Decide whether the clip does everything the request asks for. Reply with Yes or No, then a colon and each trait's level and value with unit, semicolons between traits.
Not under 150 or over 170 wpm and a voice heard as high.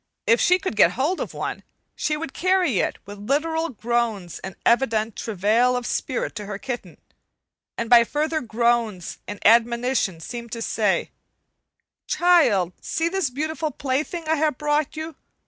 Yes: average, 155 wpm; high, 245 Hz